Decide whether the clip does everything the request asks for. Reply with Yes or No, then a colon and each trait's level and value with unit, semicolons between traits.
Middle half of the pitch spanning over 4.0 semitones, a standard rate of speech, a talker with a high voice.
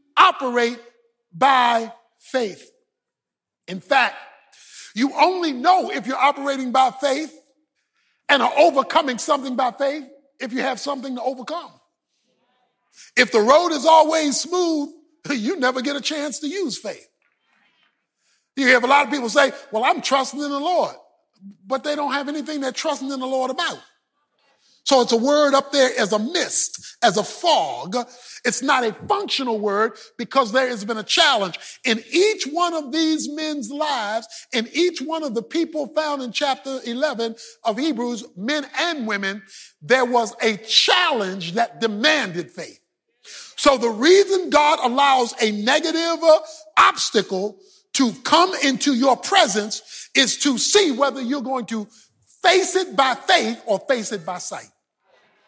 Yes: average, 4.4 semitones; average, 155 wpm; very high, 275 Hz